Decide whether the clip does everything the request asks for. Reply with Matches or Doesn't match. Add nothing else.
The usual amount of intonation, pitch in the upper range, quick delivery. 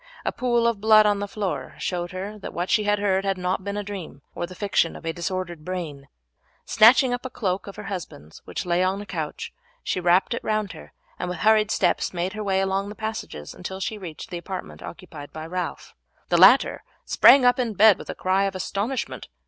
Matches